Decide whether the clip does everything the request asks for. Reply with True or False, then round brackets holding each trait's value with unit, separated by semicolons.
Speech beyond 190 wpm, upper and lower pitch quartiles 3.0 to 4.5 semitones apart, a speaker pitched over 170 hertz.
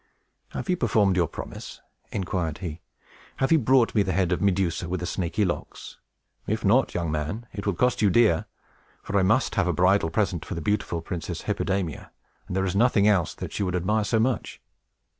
False (200 wpm; 3.4 semitones; 95 Hz)